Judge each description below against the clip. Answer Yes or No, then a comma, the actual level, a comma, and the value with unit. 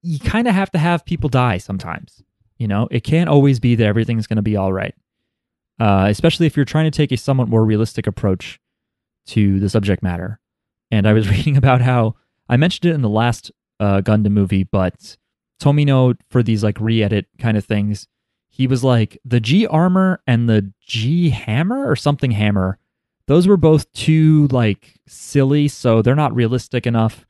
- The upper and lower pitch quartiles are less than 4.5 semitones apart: No, wide, 5.4 semitones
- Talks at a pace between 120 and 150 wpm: No, average, 190 wpm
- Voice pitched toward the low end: Yes, low, 120 Hz